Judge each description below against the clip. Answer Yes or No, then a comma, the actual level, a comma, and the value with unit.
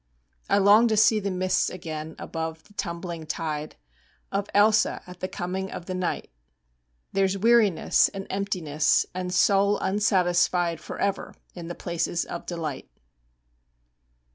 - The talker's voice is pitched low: No, medium, 185 Hz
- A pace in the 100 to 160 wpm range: Yes, slow, 135 wpm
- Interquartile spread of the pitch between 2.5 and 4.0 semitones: Yes, average, 2.9 semitones